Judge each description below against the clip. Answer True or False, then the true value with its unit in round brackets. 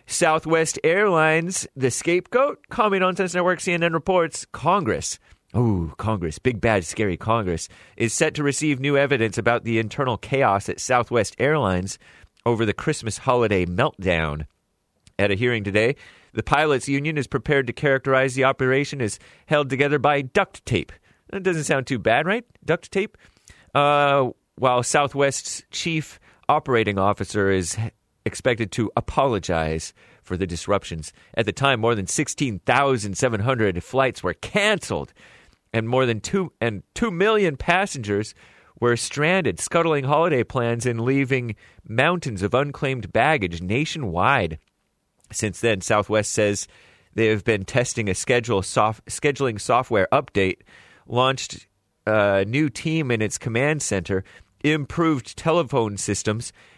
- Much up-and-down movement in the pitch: True (5.9 semitones)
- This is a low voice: True (120 Hz)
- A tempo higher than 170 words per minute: False (135 wpm)